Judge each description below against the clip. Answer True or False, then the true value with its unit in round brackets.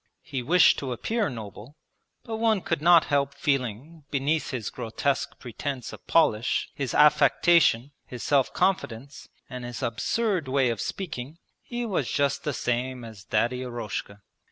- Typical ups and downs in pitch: True (4.8 semitones)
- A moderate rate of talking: True (150 wpm)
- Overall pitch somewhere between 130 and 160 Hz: True (135 Hz)